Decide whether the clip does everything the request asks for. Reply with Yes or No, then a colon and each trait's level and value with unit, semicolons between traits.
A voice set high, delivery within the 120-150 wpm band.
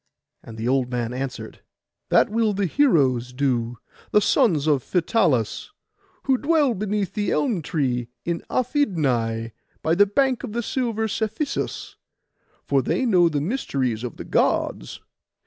No: medium, 170 Hz; average, 140 wpm